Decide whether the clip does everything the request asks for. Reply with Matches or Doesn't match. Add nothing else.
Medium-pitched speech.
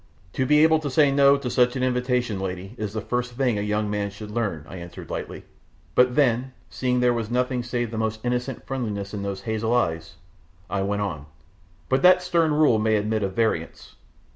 Doesn't match